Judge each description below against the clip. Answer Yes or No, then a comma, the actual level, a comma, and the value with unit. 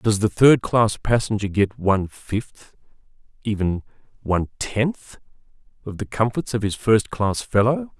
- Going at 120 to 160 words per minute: Yes, average, 145 wpm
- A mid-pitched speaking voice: No, low, 110 Hz